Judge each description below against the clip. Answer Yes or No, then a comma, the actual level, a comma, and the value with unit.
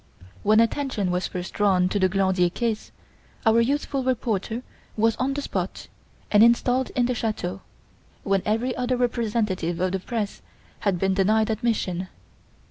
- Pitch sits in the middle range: No, high, 215 Hz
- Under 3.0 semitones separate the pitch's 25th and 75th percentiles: No, average, 4.0 semitones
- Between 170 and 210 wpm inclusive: No, average, 150 wpm